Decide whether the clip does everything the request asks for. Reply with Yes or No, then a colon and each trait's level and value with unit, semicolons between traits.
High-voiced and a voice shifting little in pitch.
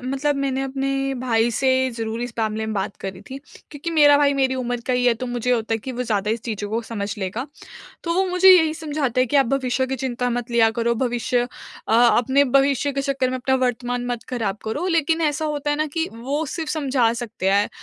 No: very high, 250 Hz; average, 3.4 semitones